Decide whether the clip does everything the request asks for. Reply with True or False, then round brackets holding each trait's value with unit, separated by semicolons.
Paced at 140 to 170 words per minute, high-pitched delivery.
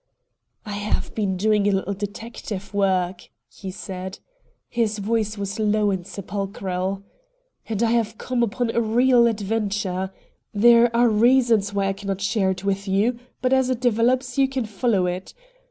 True (160 wpm; 210 Hz)